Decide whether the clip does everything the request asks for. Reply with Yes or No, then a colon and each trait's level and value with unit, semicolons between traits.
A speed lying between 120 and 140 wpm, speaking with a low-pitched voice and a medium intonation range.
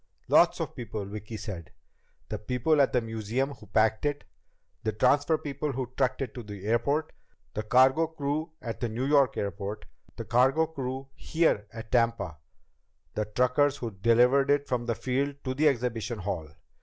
No: average, 170 wpm; low, 125 Hz; average, 4.2 semitones